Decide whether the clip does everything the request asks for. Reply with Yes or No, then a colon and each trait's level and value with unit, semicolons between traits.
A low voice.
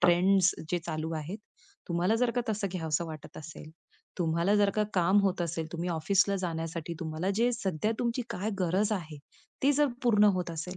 No: medium, 180 Hz